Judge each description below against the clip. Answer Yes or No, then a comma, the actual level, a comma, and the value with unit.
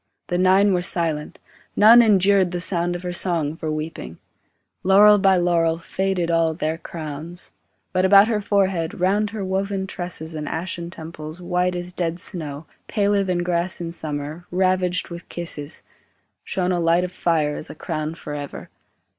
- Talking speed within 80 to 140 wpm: No, average, 165 wpm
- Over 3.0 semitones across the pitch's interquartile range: No, narrow, 2.5 semitones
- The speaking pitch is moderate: Yes, medium, 175 Hz